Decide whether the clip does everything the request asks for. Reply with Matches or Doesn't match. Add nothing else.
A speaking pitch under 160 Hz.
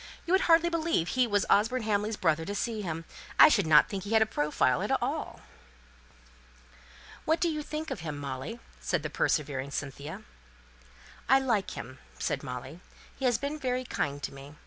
Doesn't match